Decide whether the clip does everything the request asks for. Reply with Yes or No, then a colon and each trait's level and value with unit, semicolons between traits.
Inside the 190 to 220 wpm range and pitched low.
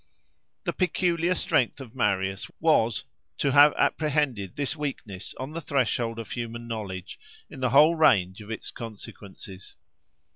No: average, 140 wpm; low, 120 Hz